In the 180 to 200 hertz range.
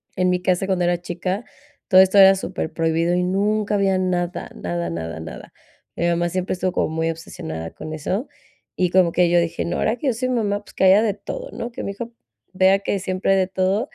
Yes: medium, 185 Hz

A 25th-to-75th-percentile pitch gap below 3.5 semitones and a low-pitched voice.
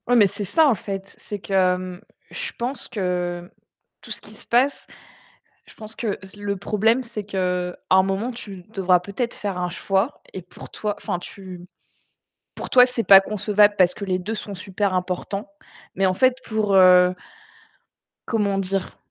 No: average, 2.8 semitones; high, 195 Hz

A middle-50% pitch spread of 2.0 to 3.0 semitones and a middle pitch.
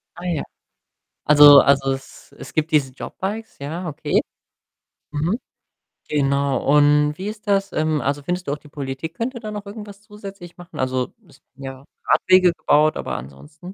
No: wide, 5.4 semitones; medium, 155 Hz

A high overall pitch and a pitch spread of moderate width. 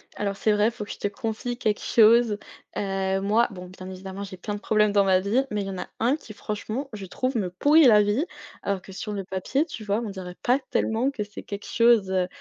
Yes: high, 205 Hz; average, 3.0 semitones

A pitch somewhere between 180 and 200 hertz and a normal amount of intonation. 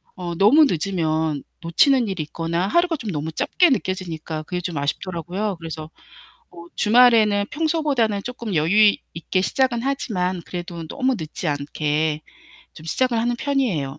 No: medium, 185 Hz; wide, 6.8 semitones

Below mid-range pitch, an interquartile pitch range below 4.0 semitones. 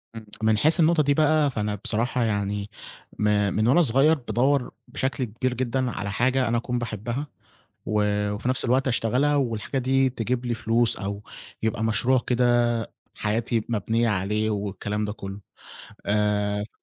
Yes: low, 115 Hz; average, 3.6 semitones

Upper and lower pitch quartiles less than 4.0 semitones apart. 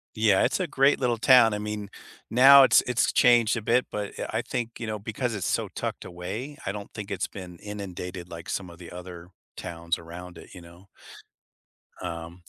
No: average, 4.7 semitones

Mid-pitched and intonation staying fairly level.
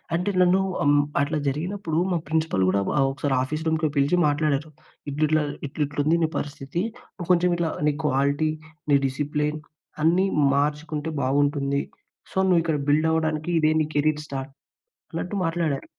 Yes: medium, 155 Hz; narrow, 2.2 semitones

